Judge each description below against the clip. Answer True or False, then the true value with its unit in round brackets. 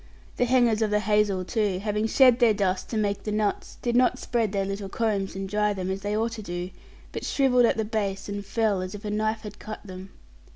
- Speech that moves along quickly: True (240 wpm)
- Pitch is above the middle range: True (210 Hz)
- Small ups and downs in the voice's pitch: True (2.2 semitones)